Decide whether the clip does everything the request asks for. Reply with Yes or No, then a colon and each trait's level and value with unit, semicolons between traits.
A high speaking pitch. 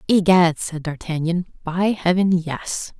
No: medium, 175 Hz